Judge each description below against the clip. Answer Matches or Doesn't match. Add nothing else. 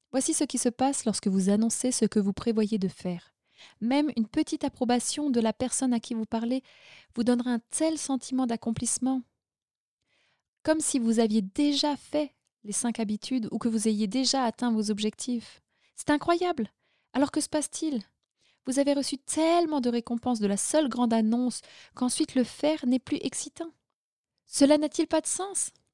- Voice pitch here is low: Doesn't match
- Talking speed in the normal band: Matches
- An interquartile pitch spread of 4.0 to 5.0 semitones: Matches